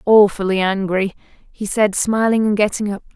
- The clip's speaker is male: No, female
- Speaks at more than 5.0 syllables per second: No, 4.8 syllables/s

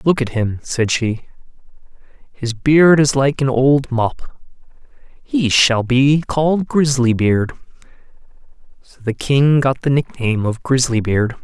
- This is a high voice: No, low, 130 Hz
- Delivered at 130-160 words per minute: Yes, average, 140 wpm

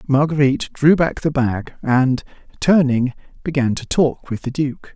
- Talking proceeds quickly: No, average, 155 wpm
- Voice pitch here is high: No, medium, 140 Hz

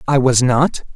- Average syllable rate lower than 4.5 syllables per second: Yes, 4.2 syllables/s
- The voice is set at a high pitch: No, low, 130 Hz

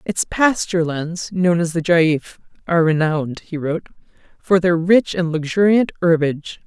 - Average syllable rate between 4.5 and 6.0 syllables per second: Yes, 5.0 syllables/s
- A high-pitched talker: No, medium, 170 Hz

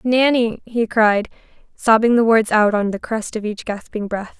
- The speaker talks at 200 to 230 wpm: No, average, 190 wpm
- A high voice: Yes, high, 220 Hz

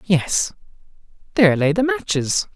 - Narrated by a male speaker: Yes, male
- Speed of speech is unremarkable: No, slow, 120 wpm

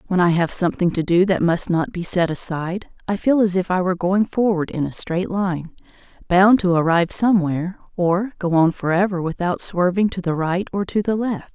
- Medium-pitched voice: Yes, medium, 180 Hz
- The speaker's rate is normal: No, fast, 215 wpm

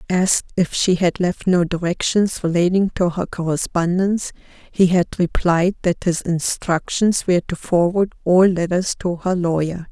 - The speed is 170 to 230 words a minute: No, average, 150 wpm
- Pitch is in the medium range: Yes, medium, 175 Hz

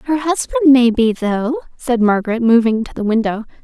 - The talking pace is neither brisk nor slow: Yes, average, 180 wpm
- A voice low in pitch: No, high, 245 Hz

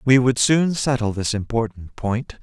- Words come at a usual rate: Yes, average, 175 wpm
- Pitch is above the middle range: No, low, 120 Hz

